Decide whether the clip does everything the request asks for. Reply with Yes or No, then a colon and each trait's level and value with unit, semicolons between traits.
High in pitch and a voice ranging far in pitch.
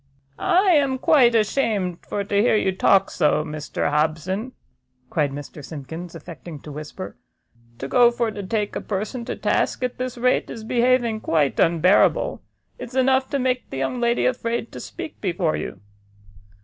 Yes: high, 215 Hz; wide, 7.4 semitones